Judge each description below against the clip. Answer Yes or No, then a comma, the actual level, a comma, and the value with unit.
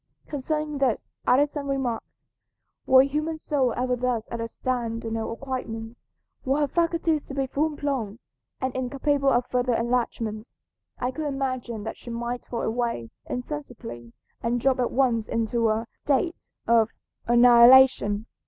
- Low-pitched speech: No, very high, 250 Hz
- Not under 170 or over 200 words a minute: No, average, 150 wpm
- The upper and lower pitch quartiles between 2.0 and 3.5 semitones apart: Yes, average, 3.1 semitones